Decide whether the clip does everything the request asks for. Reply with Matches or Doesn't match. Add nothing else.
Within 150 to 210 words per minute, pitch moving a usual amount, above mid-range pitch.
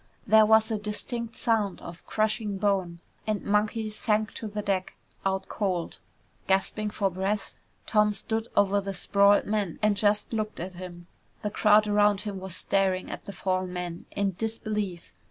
Doesn't match